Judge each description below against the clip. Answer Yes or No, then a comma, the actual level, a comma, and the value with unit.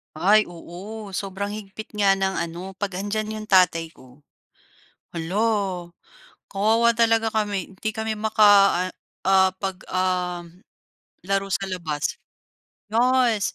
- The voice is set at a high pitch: Yes, high, 195 Hz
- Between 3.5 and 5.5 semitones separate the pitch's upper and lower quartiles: No, average, 2.8 semitones